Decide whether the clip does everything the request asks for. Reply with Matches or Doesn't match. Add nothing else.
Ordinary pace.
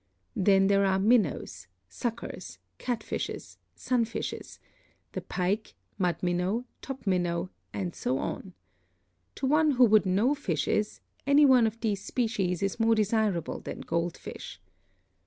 Doesn't match